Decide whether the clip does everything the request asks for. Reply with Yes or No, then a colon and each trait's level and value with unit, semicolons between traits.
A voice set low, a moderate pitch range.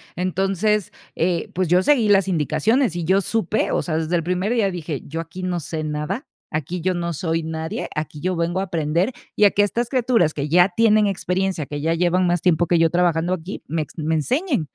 No: medium, 175 Hz; average, 3.2 semitones